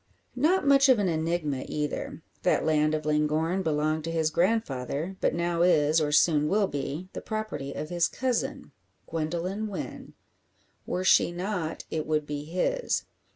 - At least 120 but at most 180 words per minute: Yes, average, 155 wpm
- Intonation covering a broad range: No, average, 3.8 semitones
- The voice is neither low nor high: Yes, medium, 165 Hz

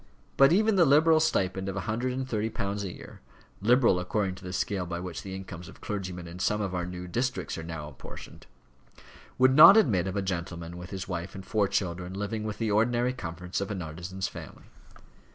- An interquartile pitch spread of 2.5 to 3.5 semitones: No, average, 4.2 semitones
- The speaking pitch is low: Yes, very low, 95 Hz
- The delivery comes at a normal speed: No, fast, 210 wpm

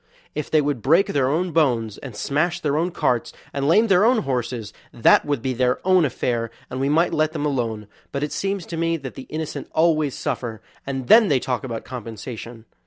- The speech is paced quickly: Yes, fast, 210 wpm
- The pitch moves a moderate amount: Yes, average, 4.8 semitones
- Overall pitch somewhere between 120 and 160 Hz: Yes, medium, 140 Hz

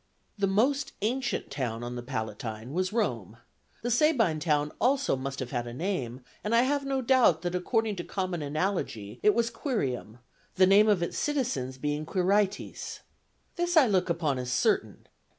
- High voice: No, medium, 180 Hz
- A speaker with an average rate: Yes, average, 170 wpm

